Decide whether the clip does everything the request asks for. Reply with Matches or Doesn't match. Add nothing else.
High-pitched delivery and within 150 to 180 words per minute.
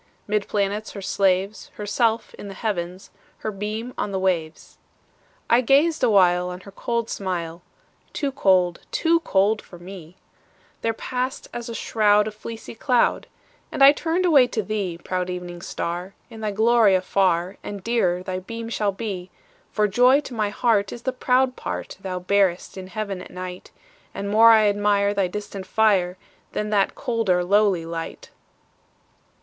Matches